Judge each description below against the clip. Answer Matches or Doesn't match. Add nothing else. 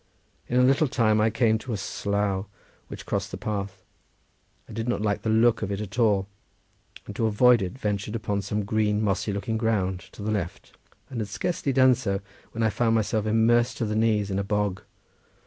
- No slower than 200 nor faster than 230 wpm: Matches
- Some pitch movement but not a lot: Doesn't match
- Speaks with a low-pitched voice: Matches